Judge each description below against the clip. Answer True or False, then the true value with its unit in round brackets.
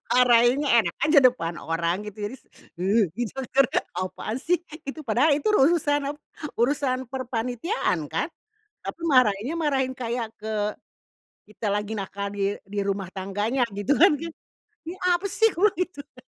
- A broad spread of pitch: True (5.8 semitones)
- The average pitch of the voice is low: False (245 Hz)